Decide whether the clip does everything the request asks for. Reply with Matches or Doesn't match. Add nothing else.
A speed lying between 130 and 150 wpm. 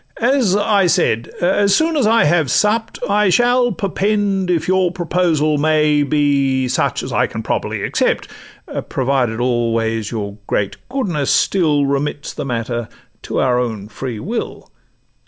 Matches